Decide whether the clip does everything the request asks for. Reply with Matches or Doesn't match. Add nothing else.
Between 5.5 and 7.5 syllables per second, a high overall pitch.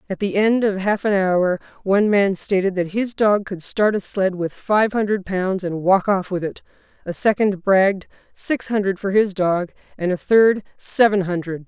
Doesn't match